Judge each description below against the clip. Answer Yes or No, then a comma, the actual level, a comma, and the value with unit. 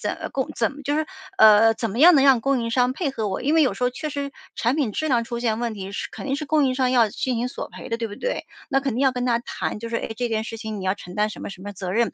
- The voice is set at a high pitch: Yes, high, 240 Hz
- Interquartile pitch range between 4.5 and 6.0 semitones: No, average, 3.8 semitones